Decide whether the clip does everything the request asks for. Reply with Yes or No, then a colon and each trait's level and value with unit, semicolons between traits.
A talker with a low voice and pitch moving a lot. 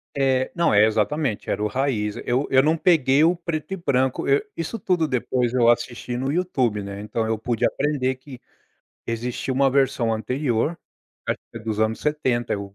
No: low, 130 Hz; average, 4.6 semitones